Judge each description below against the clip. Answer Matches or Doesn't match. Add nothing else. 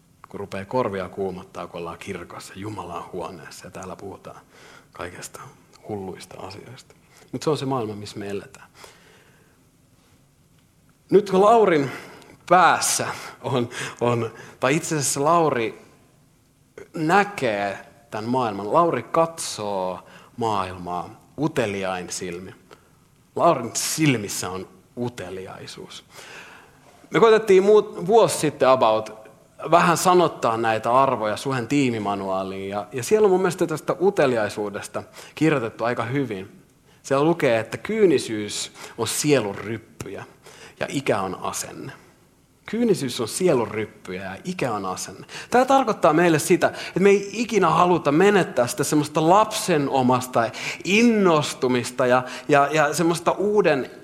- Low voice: Matches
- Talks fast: Doesn't match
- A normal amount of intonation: Doesn't match